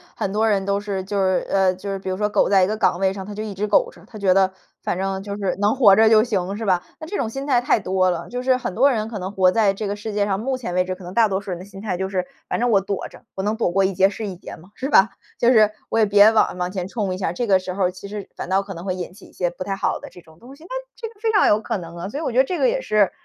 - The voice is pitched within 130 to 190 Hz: No, high, 200 Hz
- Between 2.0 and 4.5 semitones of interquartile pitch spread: Yes, average, 2.8 semitones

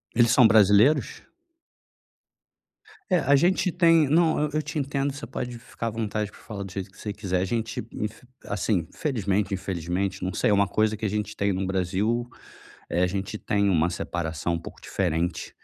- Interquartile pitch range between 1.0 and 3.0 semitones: No, average, 4.4 semitones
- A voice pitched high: No, low, 105 Hz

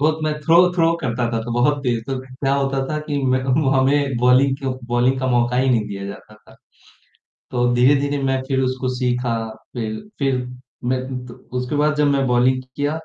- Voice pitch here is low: Yes, low, 130 Hz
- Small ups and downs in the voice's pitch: Yes, narrow, 2.3 semitones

